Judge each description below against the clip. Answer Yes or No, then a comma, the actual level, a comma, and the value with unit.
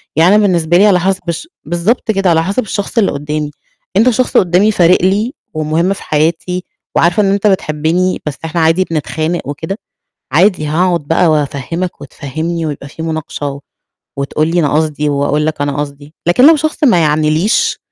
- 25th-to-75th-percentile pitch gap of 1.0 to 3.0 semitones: No, average, 3.7 semitones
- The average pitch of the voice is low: No, medium, 165 Hz